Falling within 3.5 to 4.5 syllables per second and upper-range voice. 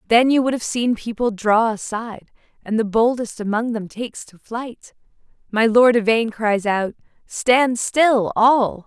Yes: 4.2 syllables/s; high, 225 Hz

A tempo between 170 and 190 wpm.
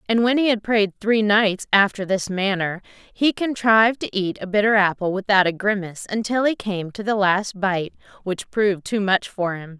No: average, 200 wpm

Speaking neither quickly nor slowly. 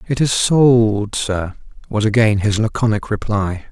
Yes: average, 145 wpm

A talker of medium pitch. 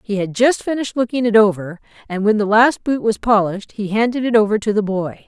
No: high, 215 Hz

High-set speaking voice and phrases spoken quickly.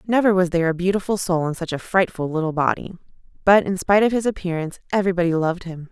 No: medium, 180 Hz; fast, 215 wpm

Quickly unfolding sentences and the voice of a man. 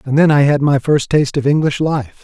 Yes: fast, 270 wpm; male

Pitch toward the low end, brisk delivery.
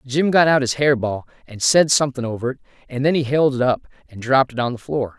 Yes: low, 130 Hz; fast, 265 wpm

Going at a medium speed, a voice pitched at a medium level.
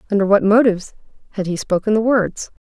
No: average, 180 wpm; high, 205 Hz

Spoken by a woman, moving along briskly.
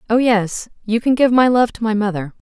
Yes: female; fast, 220 wpm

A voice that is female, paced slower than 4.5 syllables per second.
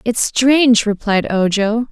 Yes: female; 3.9 syllables/s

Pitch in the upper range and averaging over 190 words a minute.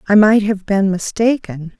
No: high, 200 Hz; average, 165 wpm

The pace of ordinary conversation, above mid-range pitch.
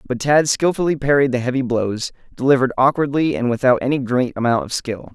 No: average, 185 wpm; low, 130 Hz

